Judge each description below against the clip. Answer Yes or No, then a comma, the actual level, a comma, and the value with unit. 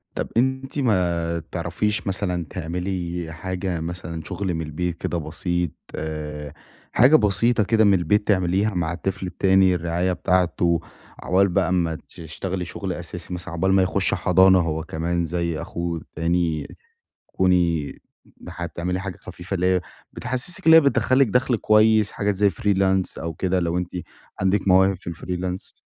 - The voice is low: Yes, very low, 90 Hz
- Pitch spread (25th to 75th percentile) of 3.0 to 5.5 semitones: No, narrow, 2.4 semitones